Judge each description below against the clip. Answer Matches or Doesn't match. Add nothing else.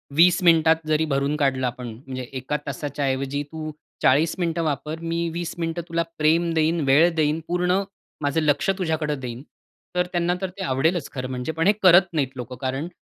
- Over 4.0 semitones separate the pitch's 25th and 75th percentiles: Doesn't match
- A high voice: Doesn't match